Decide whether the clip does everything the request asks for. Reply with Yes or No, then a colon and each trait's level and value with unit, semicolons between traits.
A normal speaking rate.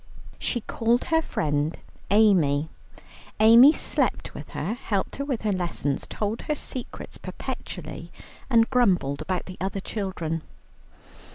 No: slow, 125 wpm